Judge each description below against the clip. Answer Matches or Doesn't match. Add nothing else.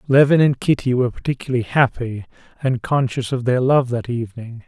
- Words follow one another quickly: Doesn't match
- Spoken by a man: Matches